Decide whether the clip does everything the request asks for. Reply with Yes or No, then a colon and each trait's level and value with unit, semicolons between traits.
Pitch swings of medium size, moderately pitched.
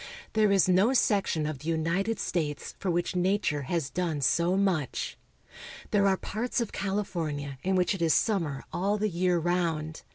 Yes: average, 3.7 semitones; medium, 180 Hz